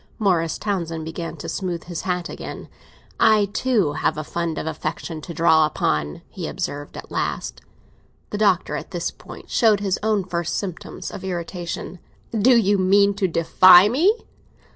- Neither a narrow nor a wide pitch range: Yes, average, 3.6 semitones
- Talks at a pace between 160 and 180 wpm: Yes, average, 165 wpm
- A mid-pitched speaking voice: Yes, medium, 180 Hz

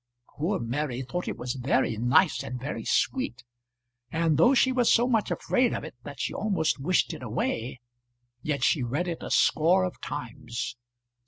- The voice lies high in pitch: No, medium, 145 Hz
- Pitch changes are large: Yes, wide, 6.1 semitones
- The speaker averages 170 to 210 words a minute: Yes, average, 175 wpm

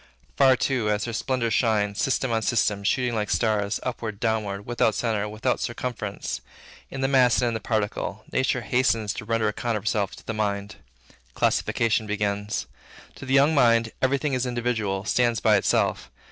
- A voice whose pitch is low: Yes, low, 115 Hz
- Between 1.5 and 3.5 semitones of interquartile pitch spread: Yes, average, 2.9 semitones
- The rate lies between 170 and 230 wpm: Yes, average, 175 wpm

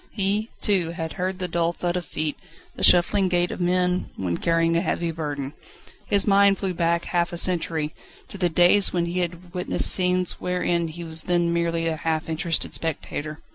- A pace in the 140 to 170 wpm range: No, average, 190 wpm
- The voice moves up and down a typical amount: No, narrow, 1.7 semitones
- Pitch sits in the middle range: Yes, medium, 175 Hz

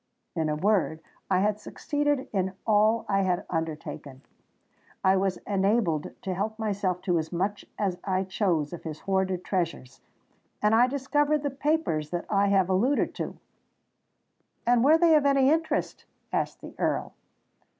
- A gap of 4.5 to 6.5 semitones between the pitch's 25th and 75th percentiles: Yes, average, 5.2 semitones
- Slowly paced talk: No, average, 150 wpm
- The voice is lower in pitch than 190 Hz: No, high, 195 Hz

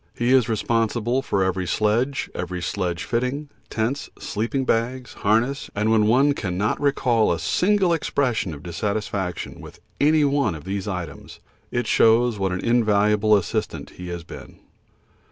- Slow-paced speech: No, average, 150 wpm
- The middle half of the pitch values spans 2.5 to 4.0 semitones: No, average, 4.9 semitones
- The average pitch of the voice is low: Yes, low, 110 Hz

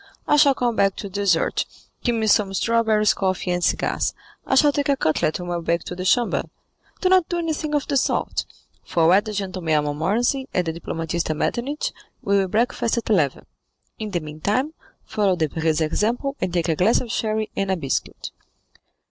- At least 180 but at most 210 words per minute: Yes, average, 195 wpm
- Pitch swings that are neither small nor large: No, wide, 5.9 semitones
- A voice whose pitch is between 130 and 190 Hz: No, high, 200 Hz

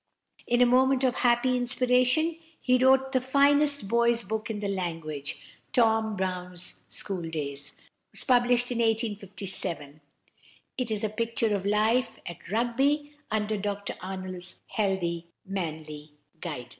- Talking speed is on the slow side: Yes, slow, 130 wpm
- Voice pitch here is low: No, high, 220 Hz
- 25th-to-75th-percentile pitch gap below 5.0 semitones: No, average, 5.3 semitones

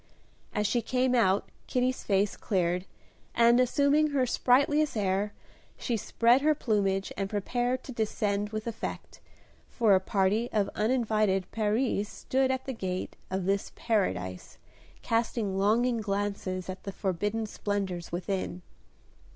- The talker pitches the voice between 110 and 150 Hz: No, high, 210 Hz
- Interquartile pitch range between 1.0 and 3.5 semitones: No, average, 3.9 semitones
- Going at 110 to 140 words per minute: Yes, slow, 135 wpm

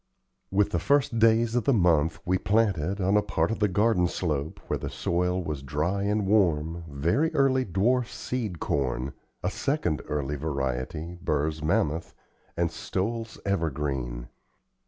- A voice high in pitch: No, very low, 90 Hz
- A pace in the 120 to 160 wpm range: Yes, average, 150 wpm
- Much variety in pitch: Yes, wide, 6.1 semitones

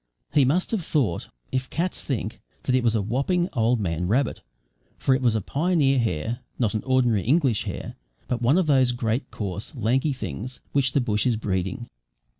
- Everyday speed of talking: Yes, average, 190 wpm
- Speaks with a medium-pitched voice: No, low, 125 Hz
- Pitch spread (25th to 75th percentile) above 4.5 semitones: No, average, 3.8 semitones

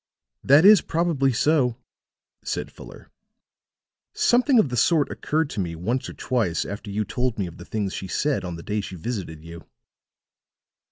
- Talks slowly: No, average, 170 wpm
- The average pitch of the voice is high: No, low, 120 Hz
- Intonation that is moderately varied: No, wide, 7.8 semitones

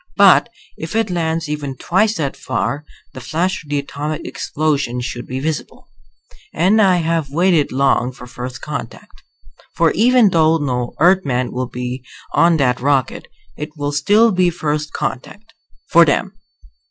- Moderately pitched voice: Yes, medium, 150 Hz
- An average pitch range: Yes, average, 4.5 semitones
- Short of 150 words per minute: No, average, 155 wpm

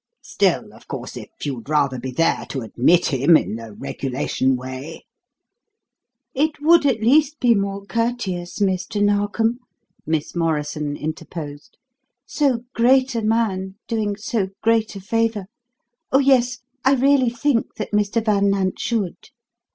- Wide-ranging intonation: Yes, wide, 7.1 semitones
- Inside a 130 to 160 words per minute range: Yes, average, 145 wpm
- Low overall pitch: No, high, 205 Hz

